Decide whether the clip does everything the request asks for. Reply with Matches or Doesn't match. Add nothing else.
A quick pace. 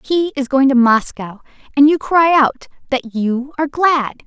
Doesn't match